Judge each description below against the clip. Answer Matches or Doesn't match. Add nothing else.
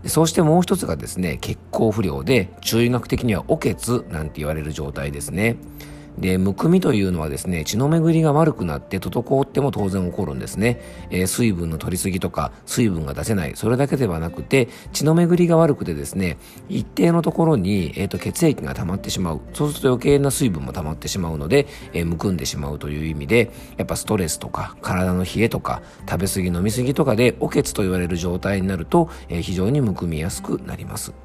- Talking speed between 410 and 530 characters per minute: Matches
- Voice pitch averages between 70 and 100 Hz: Matches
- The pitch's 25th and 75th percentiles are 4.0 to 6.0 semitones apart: Doesn't match